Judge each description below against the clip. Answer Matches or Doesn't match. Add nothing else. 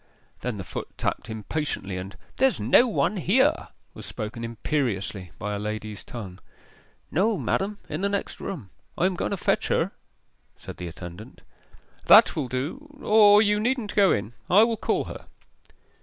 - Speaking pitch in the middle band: Matches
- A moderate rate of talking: Matches